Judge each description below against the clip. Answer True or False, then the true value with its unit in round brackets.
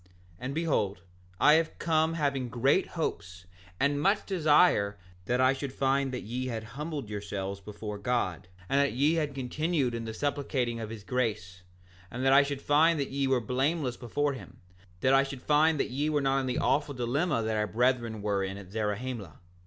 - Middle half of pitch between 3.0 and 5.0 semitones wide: True (4.5 semitones)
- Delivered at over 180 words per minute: True (190 wpm)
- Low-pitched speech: True (130 Hz)